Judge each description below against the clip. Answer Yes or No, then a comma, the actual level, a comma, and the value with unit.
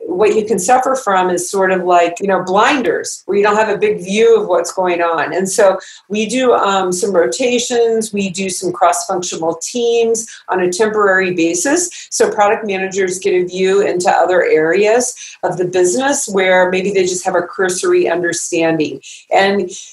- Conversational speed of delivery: Yes, average, 180 wpm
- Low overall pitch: No, high, 190 Hz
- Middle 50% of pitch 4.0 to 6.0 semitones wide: No, average, 3.6 semitones